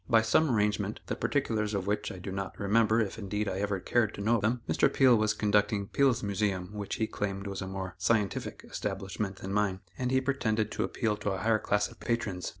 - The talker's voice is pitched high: No, low, 105 Hz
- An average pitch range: No, narrow, 2.3 semitones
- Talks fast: Yes, fast, 220 wpm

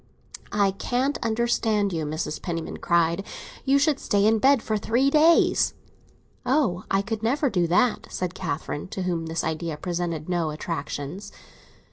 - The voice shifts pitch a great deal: Yes, wide, 6.0 semitones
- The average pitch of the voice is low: No, high, 195 Hz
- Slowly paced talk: No, average, 150 wpm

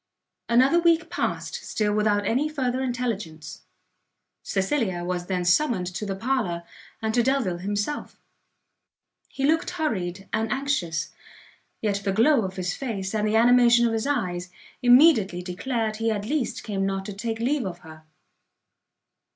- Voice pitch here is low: No, high, 220 Hz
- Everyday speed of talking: Yes, average, 150 wpm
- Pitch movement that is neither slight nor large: Yes, average, 5.0 semitones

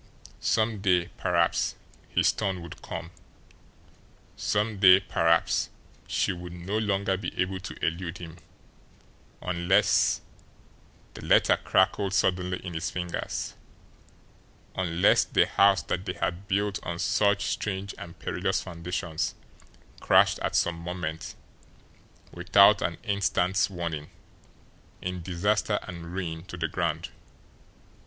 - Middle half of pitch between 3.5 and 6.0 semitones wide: No, narrow, 2.5 semitones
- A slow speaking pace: Yes, slow, 120 wpm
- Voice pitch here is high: No, very low, 90 Hz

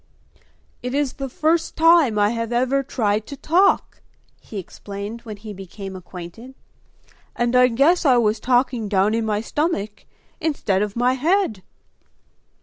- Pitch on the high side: Yes, high, 235 Hz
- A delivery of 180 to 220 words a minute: No, average, 145 wpm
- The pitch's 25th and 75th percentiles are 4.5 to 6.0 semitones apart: Yes, average, 4.8 semitones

